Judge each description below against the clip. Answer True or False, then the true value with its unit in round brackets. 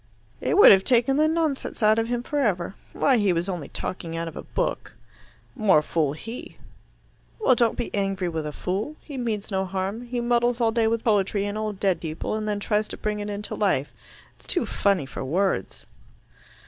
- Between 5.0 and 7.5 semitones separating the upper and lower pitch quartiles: False (4.0 semitones)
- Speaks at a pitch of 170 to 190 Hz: False (210 Hz)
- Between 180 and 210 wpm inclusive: True (205 wpm)